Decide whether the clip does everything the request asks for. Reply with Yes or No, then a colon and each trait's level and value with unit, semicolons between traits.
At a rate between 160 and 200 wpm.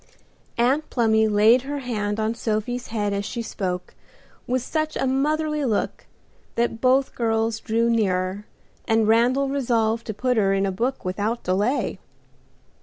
No: average, 150 wpm